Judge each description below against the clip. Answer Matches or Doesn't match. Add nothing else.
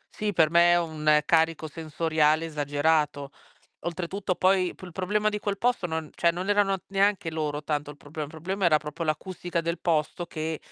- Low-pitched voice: Doesn't match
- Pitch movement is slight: Doesn't match